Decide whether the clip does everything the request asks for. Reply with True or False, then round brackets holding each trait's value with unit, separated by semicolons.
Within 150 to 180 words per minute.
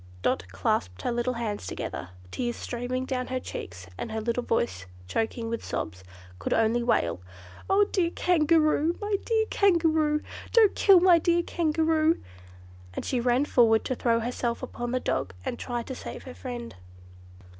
True (165 wpm)